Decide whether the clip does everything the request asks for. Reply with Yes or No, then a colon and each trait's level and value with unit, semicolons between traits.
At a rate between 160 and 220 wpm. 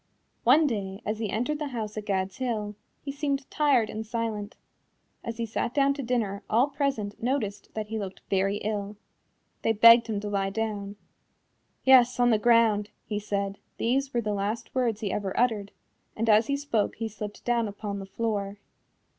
Yes: average, 185 wpm